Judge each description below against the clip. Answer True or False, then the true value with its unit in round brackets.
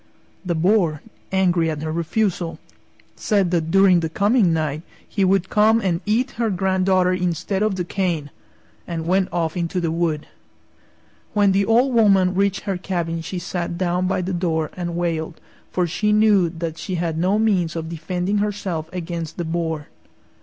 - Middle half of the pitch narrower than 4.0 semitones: True (2.8 semitones)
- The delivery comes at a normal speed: True (170 wpm)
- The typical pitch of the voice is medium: True (180 Hz)